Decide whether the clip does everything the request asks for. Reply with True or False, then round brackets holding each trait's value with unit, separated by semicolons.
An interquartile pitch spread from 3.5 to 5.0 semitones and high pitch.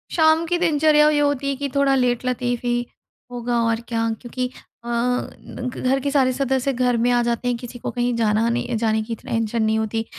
False (2.7 semitones; 245 Hz)